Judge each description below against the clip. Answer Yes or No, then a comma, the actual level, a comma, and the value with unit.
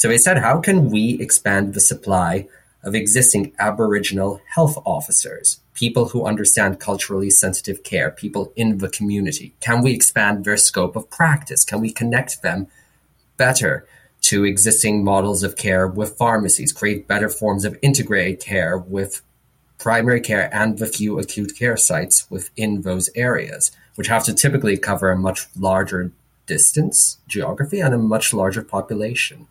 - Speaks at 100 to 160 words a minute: Yes, average, 155 wpm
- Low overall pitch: Yes, low, 105 Hz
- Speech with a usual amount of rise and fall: Yes, average, 3.6 semitones